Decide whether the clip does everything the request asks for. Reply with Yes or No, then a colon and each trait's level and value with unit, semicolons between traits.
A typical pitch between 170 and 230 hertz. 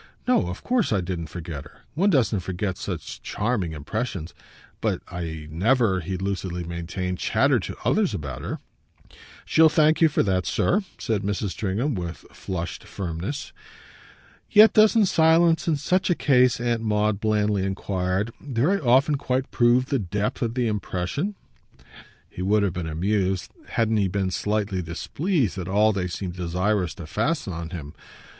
No: low, 100 Hz